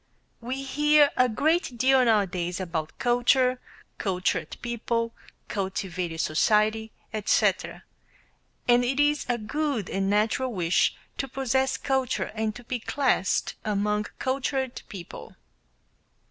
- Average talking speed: No, slow, 120 wpm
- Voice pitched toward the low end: No, high, 235 Hz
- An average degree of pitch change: Yes, average, 4.4 semitones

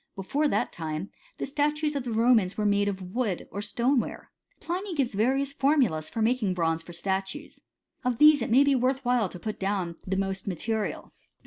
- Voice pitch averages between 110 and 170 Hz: No, high, 225 Hz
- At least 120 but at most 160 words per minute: No, average, 190 wpm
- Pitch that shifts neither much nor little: No, wide, 6.0 semitones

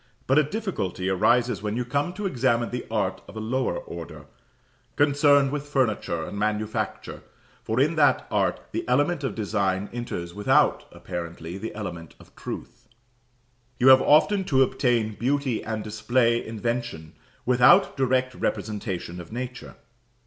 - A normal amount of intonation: Yes, average, 4.4 semitones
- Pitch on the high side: No, low, 120 Hz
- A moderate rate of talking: Yes, average, 145 wpm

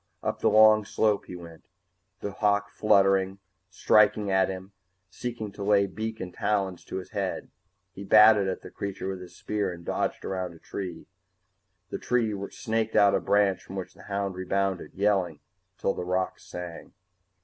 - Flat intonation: Yes, narrow, 2.0 semitones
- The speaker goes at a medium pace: Yes, average, 170 wpm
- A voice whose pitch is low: Yes, low, 100 Hz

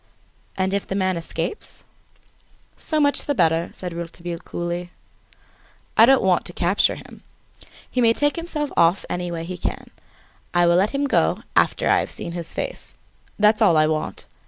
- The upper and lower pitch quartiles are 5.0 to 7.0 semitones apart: Yes, wide, 5.4 semitones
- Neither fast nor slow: Yes, average, 175 wpm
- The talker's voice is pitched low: No, medium, 185 Hz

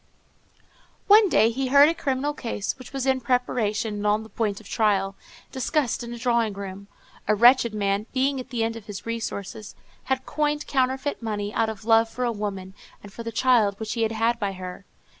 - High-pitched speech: Yes, high, 230 Hz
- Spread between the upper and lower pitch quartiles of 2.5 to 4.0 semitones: Yes, average, 3.7 semitones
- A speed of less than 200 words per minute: No, fast, 205 wpm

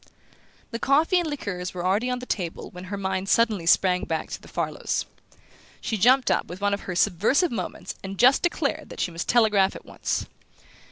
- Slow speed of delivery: No, average, 190 wpm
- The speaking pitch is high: Yes, high, 200 Hz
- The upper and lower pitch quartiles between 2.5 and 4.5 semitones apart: No, average, 5.3 semitones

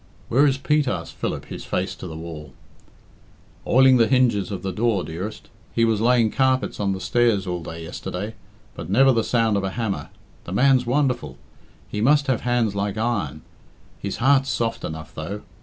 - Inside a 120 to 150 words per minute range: No, average, 185 wpm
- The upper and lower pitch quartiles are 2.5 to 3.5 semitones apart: No, average, 5.1 semitones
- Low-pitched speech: Yes, low, 110 Hz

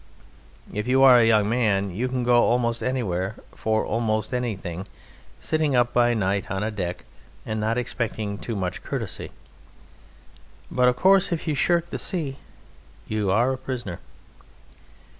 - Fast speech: No, average, 150 wpm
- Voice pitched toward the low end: Yes, low, 115 Hz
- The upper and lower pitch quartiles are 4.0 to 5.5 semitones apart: No, average, 3.5 semitones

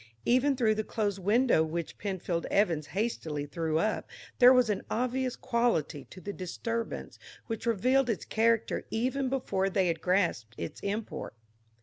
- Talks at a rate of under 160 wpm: Yes, average, 150 wpm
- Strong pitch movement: Yes, wide, 5.8 semitones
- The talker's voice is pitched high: Yes, high, 210 Hz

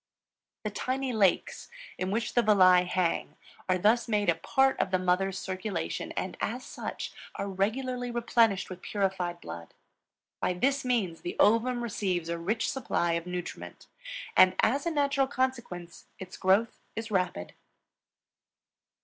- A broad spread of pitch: No, average, 4.8 semitones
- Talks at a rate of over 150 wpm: No, average, 145 wpm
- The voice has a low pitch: No, high, 200 Hz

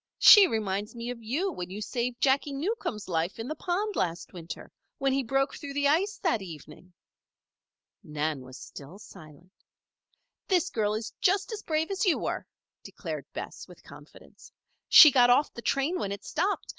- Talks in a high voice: Yes, high, 245 Hz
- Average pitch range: No, wide, 8.6 semitones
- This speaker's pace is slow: No, average, 175 wpm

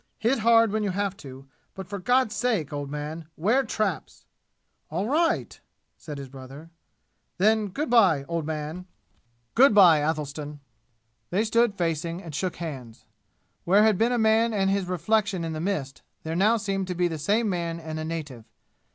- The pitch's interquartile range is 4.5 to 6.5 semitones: Yes, wide, 5.6 semitones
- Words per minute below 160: No, average, 175 wpm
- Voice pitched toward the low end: No, medium, 180 Hz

